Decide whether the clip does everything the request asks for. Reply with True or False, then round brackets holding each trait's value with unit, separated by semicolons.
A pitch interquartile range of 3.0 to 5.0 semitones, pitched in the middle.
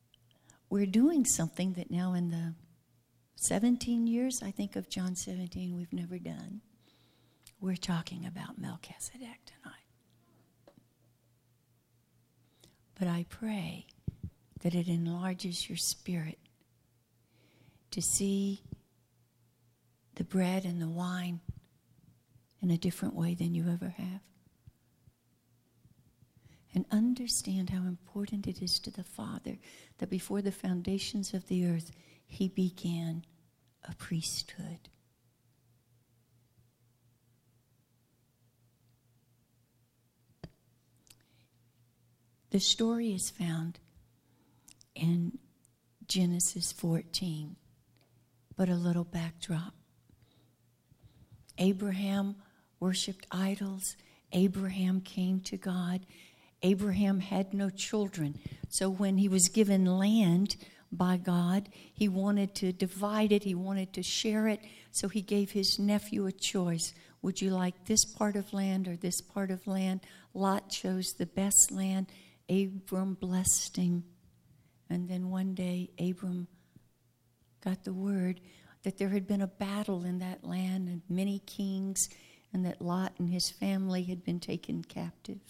True (4.2 semitones; 180 Hz)